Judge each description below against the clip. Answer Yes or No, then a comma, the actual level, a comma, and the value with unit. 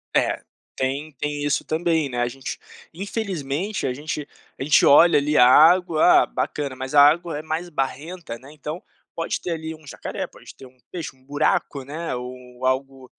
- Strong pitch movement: No, average, 3.6 semitones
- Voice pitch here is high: No, medium, 145 Hz